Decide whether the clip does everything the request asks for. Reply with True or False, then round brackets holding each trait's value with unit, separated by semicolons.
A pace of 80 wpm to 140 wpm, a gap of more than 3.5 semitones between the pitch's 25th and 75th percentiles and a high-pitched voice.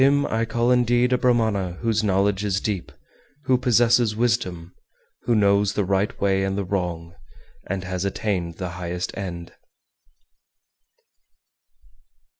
False (135 wpm; 4.2 semitones; 100 Hz)